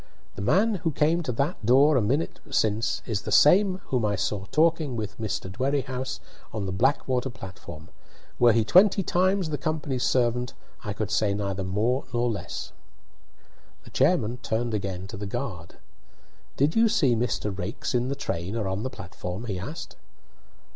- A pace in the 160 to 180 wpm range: Yes, average, 170 wpm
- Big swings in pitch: Yes, wide, 5.9 semitones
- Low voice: Yes, low, 120 Hz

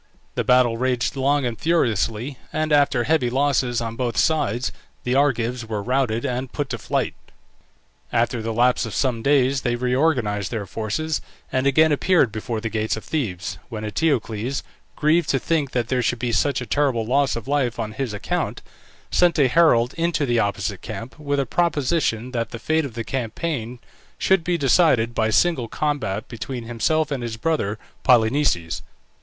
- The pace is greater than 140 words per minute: Yes, average, 175 wpm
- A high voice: No, low, 125 Hz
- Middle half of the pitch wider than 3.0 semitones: Yes, average, 4.1 semitones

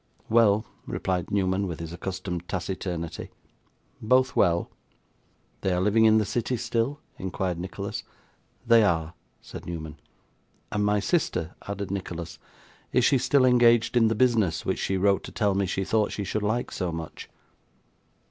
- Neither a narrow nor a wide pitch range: Yes, average, 4.1 semitones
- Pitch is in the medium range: No, low, 100 Hz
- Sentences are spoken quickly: No, average, 155 wpm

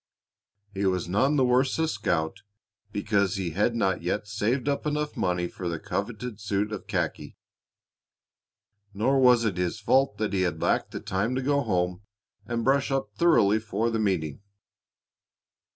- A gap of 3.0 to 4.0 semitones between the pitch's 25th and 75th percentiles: No, average, 5.2 semitones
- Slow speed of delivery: No, average, 165 wpm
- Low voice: Yes, low, 105 Hz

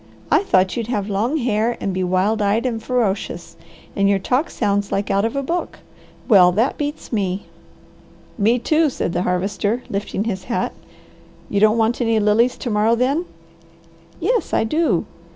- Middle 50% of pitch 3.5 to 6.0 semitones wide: Yes, average, 3.9 semitones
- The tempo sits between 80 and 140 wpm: No, average, 170 wpm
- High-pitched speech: Yes, high, 220 Hz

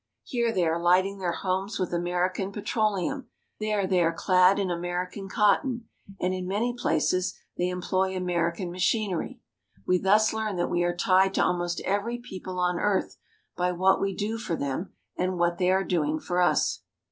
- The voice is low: No, medium, 185 Hz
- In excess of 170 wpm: Yes, average, 180 wpm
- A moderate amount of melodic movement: No, narrow, 2.3 semitones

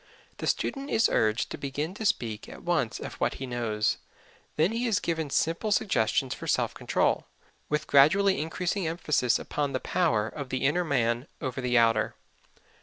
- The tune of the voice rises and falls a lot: Yes, wide, 6.4 semitones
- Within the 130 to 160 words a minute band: No, average, 175 wpm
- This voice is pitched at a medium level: Yes, medium, 145 Hz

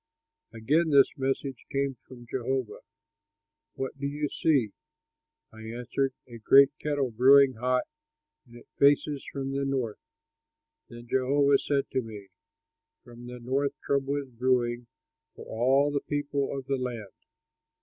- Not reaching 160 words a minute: Yes, average, 140 wpm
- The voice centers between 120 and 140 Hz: Yes, low, 135 Hz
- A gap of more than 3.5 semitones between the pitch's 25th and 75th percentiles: No, narrow, 2.5 semitones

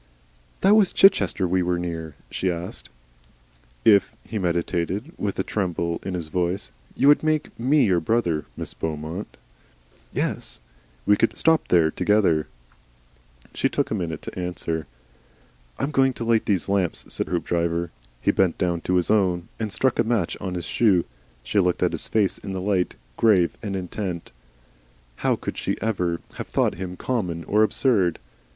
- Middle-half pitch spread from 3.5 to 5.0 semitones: Yes, average, 4.0 semitones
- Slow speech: No, average, 170 wpm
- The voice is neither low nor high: No, very low, 90 Hz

